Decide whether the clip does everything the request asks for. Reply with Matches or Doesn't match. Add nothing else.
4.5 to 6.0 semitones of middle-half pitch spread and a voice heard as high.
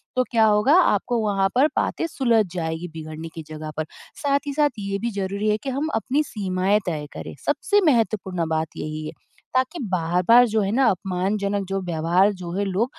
Matches